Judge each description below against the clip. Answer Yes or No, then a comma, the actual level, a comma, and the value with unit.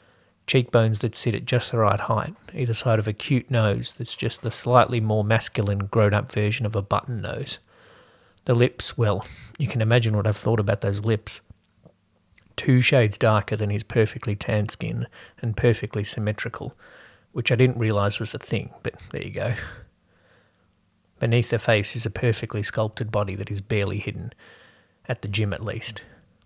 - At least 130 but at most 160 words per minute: No, average, 175 wpm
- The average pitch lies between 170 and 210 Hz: No, low, 110 Hz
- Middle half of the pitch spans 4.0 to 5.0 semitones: No, narrow, 2.5 semitones